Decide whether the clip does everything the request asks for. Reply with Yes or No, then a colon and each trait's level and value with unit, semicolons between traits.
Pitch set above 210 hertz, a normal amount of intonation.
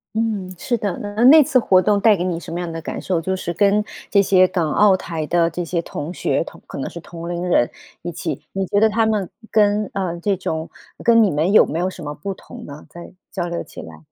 No: medium, 185 Hz; average, 3.4 semitones